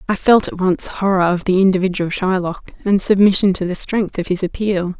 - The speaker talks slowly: No, fast, 205 wpm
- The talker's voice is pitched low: No, high, 190 Hz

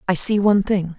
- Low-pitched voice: No, high, 190 Hz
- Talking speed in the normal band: No, fast, 245 wpm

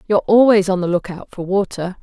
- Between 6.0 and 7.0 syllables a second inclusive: Yes, 6.2 syllables/s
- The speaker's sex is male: No, female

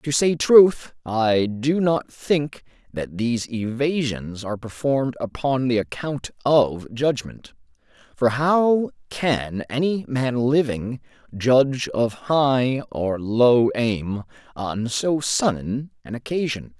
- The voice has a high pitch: No, low, 125 Hz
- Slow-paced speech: Yes, slow, 120 wpm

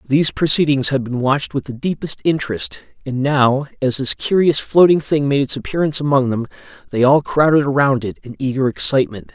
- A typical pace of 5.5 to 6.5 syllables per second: Yes, 5.7 syllables/s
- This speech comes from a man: Yes, male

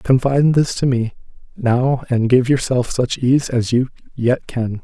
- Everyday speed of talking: Yes, average, 175 wpm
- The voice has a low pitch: Yes, low, 125 Hz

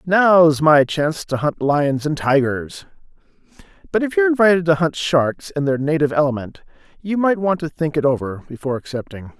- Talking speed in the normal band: Yes, average, 180 wpm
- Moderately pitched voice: Yes, medium, 155 Hz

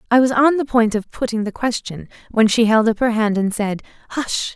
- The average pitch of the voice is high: Yes, high, 230 Hz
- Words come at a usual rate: No, fast, 235 wpm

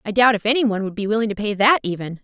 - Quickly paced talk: Yes, fast, 320 wpm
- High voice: Yes, high, 215 Hz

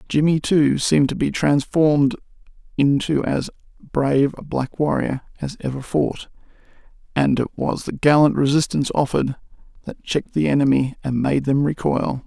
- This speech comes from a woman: No, male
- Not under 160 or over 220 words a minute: No, average, 145 wpm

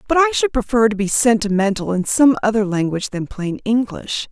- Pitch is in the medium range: No, high, 220 Hz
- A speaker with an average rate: Yes, average, 195 wpm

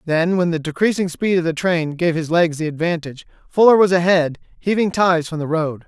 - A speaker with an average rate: No, fast, 215 wpm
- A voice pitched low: No, medium, 170 Hz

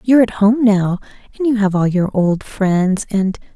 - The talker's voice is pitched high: Yes, high, 205 Hz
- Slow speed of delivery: No, fast, 205 wpm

